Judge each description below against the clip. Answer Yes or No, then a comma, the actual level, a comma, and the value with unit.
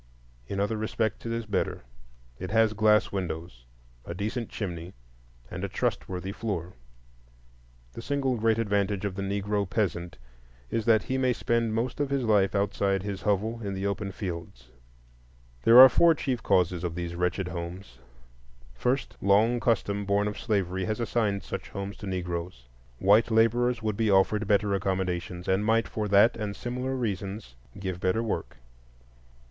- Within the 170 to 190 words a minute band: No, average, 160 wpm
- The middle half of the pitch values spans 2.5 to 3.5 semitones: Yes, average, 3.2 semitones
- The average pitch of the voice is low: Yes, low, 100 Hz